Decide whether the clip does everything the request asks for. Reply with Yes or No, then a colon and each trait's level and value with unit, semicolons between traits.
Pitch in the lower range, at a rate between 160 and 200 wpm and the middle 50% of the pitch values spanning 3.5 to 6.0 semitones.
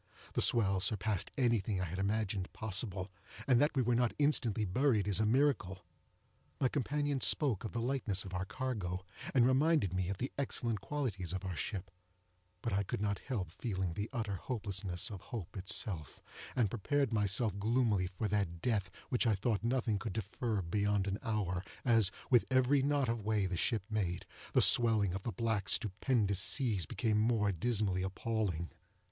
Yes: low, 105 Hz; average, 175 wpm; average, 4.1 semitones